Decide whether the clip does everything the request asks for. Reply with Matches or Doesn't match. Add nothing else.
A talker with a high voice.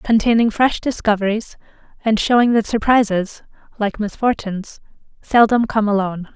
Matches